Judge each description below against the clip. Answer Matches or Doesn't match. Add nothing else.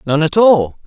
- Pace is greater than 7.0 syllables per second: Doesn't match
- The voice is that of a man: Matches